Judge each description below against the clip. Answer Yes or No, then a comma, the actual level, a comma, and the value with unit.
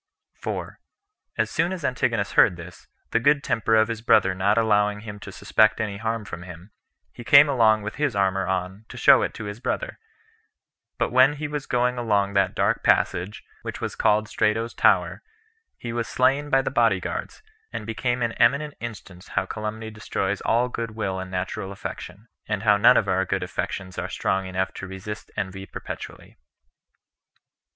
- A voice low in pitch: Yes, low, 105 Hz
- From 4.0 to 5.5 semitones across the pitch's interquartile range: No, average, 3.5 semitones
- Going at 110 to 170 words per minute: No, average, 180 wpm